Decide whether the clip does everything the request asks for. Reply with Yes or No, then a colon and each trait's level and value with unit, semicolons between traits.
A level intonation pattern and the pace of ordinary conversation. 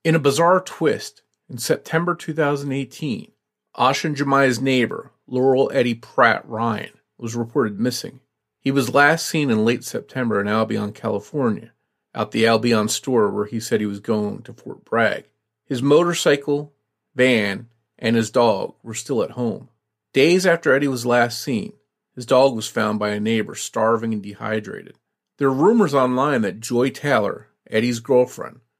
No: average, 4.3 semitones; average, 160 wpm